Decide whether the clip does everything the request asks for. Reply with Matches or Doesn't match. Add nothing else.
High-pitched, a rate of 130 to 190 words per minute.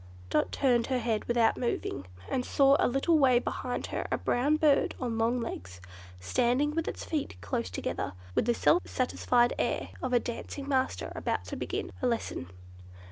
Matches